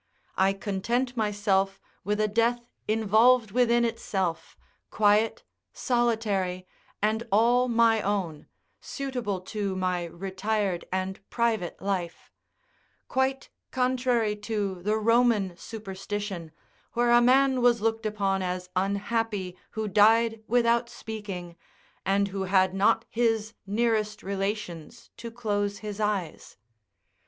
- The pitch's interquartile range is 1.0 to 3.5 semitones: Yes, average, 3.2 semitones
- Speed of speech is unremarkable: No, slow, 110 wpm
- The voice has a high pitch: Yes, high, 210 Hz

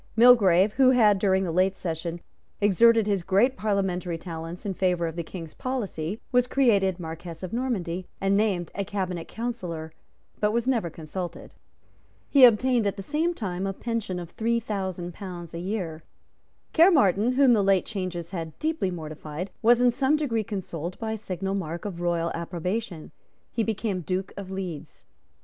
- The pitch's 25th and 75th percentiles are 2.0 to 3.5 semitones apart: No, average, 4.5 semitones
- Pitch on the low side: No, high, 195 Hz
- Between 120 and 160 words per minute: No, average, 170 wpm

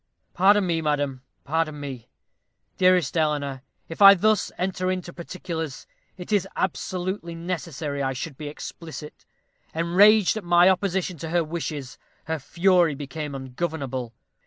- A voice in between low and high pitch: Yes, medium, 165 Hz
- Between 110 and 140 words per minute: Yes, slow, 135 wpm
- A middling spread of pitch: Yes, average, 4.0 semitones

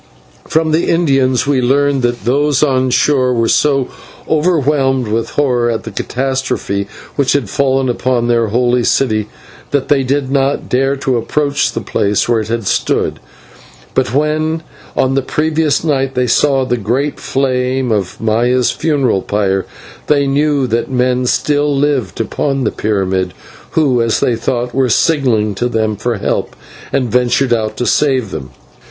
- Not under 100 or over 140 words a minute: No, average, 160 wpm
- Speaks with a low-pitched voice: Yes, low, 130 Hz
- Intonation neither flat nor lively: Yes, average, 3.2 semitones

